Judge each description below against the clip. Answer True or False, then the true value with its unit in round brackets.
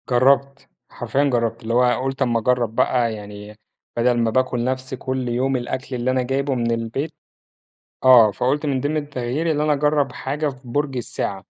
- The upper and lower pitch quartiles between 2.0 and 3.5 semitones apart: True (2.6 semitones)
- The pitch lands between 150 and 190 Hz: False (130 Hz)